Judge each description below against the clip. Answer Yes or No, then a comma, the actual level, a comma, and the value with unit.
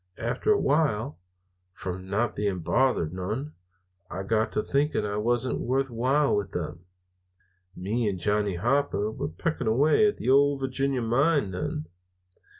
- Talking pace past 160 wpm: No, average, 150 wpm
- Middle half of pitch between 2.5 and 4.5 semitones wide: No, wide, 5.4 semitones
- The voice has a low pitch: Yes, low, 120 Hz